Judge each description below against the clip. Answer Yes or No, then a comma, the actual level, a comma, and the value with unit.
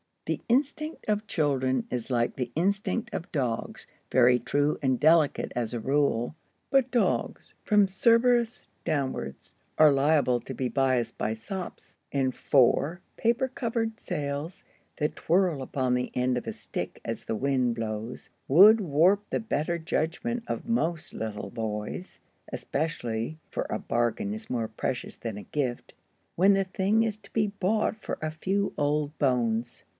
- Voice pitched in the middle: Yes, medium, 150 Hz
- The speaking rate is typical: Yes, average, 155 wpm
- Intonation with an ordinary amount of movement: No, wide, 8.2 semitones